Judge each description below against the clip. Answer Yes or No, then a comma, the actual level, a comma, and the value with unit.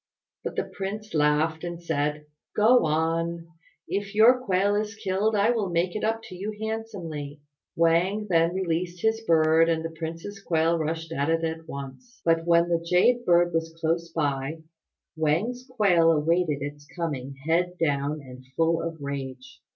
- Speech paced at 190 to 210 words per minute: No, average, 165 wpm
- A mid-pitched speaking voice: Yes, medium, 165 Hz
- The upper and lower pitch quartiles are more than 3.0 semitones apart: Yes, average, 3.7 semitones